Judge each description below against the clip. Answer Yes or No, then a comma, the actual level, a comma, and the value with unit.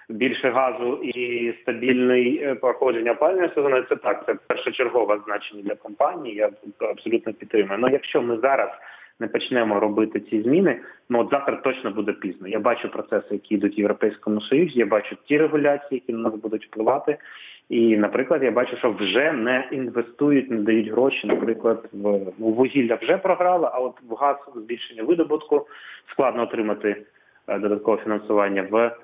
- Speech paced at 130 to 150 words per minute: No, average, 160 wpm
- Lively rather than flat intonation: No, average, 3.8 semitones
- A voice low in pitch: Yes, low, 115 Hz